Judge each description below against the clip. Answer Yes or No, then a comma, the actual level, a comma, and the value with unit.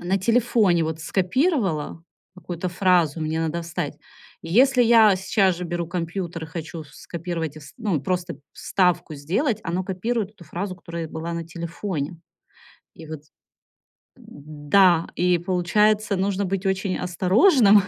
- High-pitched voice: No, medium, 180 Hz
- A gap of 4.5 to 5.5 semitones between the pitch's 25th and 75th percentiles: No, average, 3.2 semitones